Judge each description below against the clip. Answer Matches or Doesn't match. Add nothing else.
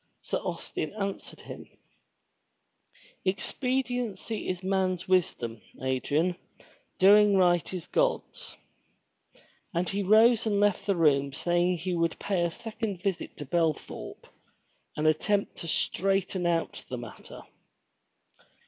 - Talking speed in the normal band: Doesn't match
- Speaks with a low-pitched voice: Doesn't match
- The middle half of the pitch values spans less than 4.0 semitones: Matches